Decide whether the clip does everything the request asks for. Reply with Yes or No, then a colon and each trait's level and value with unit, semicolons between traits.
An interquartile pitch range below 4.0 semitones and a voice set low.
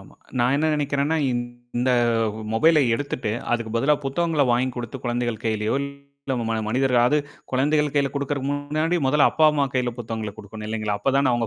Yes: average, 3.6 semitones; low, 130 Hz